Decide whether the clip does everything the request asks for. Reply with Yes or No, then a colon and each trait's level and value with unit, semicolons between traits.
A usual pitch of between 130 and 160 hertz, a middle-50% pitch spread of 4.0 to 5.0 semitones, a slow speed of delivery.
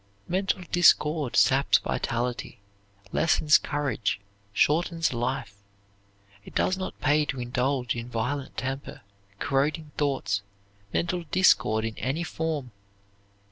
Yes: medium, 140 Hz; average, 4.5 semitones; slow, 105 wpm